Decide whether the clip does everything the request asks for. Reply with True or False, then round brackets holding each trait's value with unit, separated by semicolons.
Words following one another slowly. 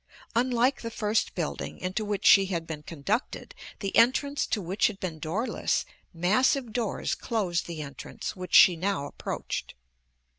False (150 wpm)